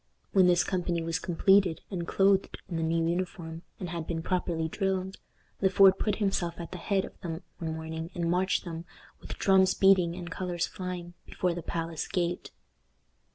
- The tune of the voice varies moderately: No, narrow, 2.2 semitones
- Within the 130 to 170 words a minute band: No, average, 180 wpm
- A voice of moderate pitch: Yes, medium, 175 Hz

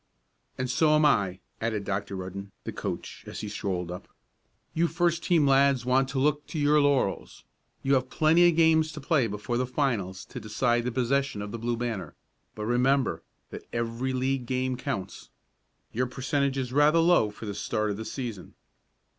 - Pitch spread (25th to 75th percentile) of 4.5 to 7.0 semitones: Yes, average, 4.8 semitones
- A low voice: Yes, low, 125 Hz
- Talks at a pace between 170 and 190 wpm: Yes, average, 185 wpm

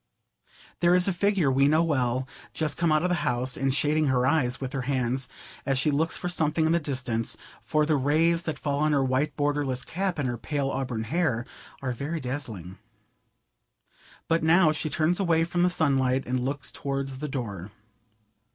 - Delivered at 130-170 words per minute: No, average, 190 wpm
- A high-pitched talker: No, medium, 145 Hz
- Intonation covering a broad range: No, average, 3.7 semitones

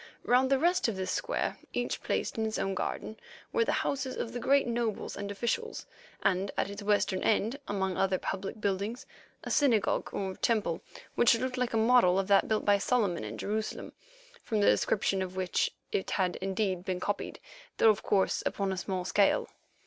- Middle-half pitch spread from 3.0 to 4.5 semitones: Yes, average, 3.7 semitones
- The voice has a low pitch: No, high, 205 Hz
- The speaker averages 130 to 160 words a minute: No, average, 190 wpm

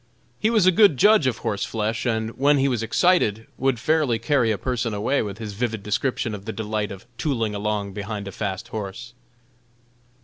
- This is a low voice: Yes, low, 115 Hz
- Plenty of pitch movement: No, average, 4.1 semitones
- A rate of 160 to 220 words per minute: Yes, average, 190 wpm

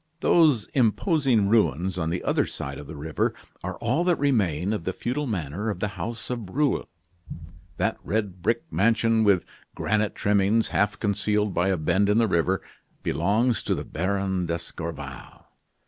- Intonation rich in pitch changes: No, average, 4.4 semitones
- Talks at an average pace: Yes, average, 160 wpm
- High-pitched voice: No, low, 100 Hz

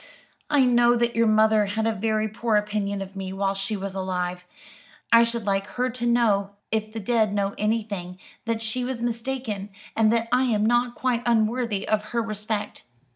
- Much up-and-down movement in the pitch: No, narrow, 2.6 semitones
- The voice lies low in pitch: No, high, 220 Hz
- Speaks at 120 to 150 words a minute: No, average, 185 wpm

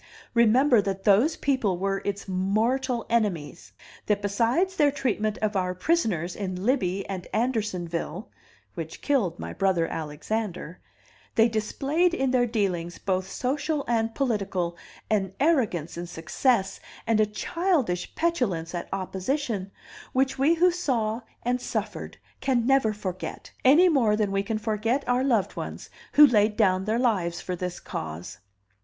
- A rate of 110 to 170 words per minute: Yes, average, 145 wpm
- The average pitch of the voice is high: Yes, high, 215 Hz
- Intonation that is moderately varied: No, wide, 5.7 semitones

